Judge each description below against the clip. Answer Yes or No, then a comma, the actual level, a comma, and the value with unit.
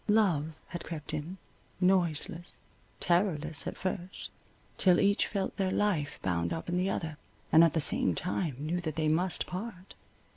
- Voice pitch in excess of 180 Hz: No, medium, 175 Hz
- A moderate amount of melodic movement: Yes, average, 3.1 semitones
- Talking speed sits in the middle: Yes, average, 160 wpm